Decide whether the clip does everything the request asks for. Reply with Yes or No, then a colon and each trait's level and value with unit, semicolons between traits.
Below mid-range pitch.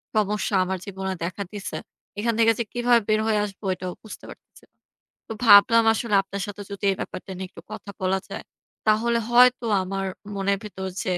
No: high, 205 Hz